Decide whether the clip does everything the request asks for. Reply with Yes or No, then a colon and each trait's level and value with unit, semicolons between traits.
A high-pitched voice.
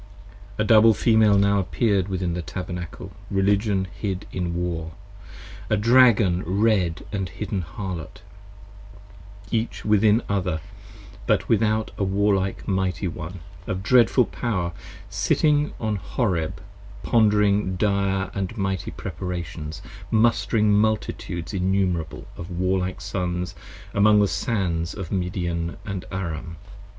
No: very low, 95 Hz